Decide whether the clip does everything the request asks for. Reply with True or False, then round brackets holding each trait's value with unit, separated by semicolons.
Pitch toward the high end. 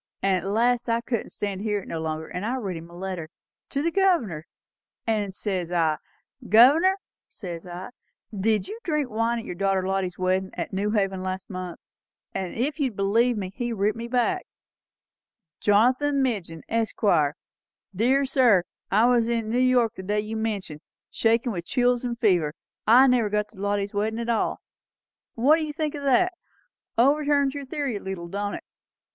True (220 Hz)